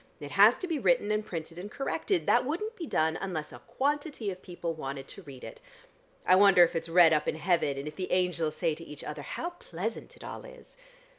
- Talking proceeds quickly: Yes, fast, 230 wpm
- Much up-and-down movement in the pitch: Yes, wide, 8.3 semitones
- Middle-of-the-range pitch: Yes, medium, 180 Hz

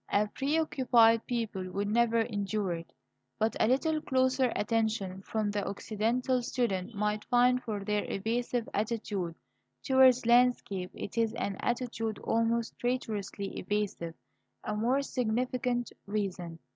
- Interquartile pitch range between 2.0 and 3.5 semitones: Yes, average, 3.2 semitones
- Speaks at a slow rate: Yes, slow, 125 wpm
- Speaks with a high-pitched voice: Yes, high, 225 Hz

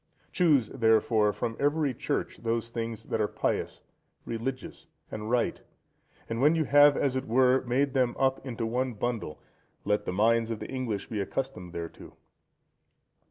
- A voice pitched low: Yes, low, 120 Hz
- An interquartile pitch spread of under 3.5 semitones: Yes, average, 3.0 semitones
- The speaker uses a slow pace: No, average, 160 wpm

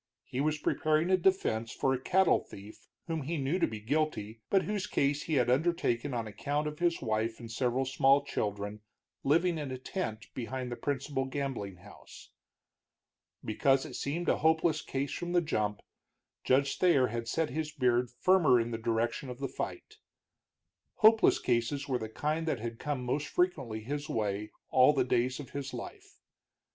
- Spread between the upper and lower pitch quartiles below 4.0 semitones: No, average, 4.7 semitones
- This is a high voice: No, low, 135 Hz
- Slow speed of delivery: No, average, 175 wpm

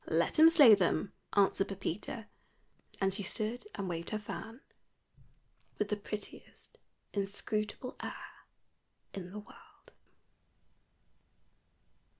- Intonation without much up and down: Yes, narrow, 2.0 semitones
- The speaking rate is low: Yes, slow, 105 wpm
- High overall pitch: Yes, high, 205 Hz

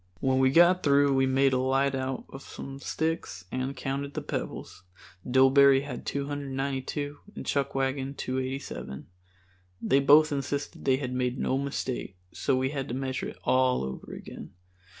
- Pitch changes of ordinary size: No, narrow, 1.2 semitones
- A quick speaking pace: No, average, 155 wpm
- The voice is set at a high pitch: No, low, 135 Hz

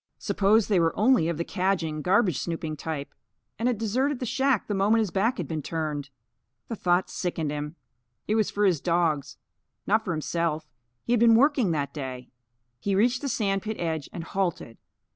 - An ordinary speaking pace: Yes, average, 190 wpm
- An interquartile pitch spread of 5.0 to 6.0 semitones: Yes, wide, 5.6 semitones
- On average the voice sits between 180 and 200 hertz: Yes, medium, 185 Hz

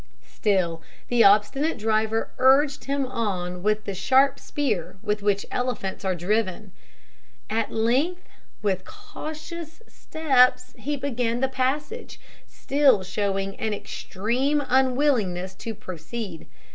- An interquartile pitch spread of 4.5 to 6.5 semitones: Yes, wide, 5.5 semitones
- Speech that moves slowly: Yes, slow, 115 wpm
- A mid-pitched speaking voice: No, high, 230 Hz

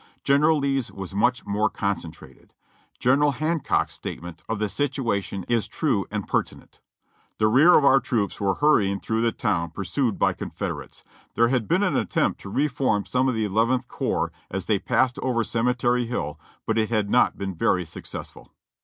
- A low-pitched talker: Yes, low, 115 Hz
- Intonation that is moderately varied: Yes, average, 4.8 semitones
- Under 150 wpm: No, average, 170 wpm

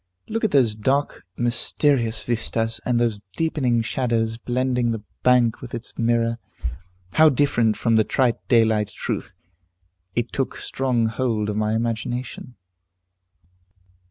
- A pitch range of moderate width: No, narrow, 2.2 semitones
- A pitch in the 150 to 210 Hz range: No, low, 120 Hz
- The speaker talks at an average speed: No, slow, 130 wpm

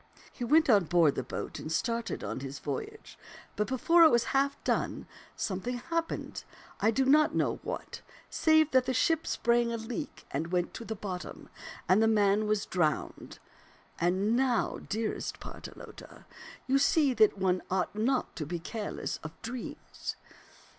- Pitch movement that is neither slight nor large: No, wide, 6.0 semitones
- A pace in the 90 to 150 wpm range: No, average, 160 wpm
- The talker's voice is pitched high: Yes, high, 225 Hz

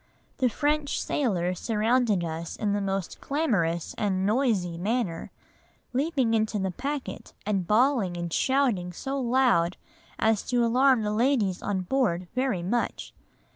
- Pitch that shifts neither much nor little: No, wide, 5.8 semitones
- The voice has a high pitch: Yes, high, 220 Hz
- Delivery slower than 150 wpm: Yes, slow, 135 wpm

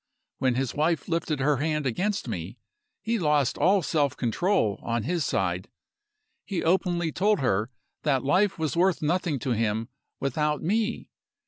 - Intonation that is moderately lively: No, wide, 5.9 semitones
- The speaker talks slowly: No, average, 150 wpm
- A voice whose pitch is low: No, medium, 150 Hz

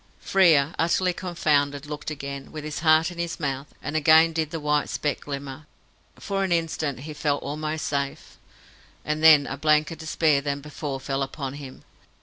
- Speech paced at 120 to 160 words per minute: No, average, 170 wpm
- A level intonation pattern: Yes, narrow, 2.2 semitones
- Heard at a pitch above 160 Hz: No, medium, 150 Hz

